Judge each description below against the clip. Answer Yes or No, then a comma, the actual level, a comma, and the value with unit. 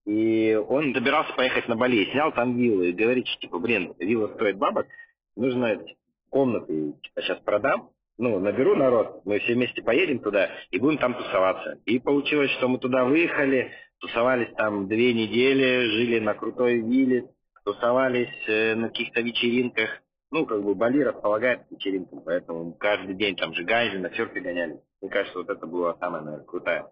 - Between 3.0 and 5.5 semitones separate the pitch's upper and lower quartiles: Yes, average, 3.3 semitones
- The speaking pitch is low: Yes, low, 120 Hz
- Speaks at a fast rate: Yes, fast, 165 wpm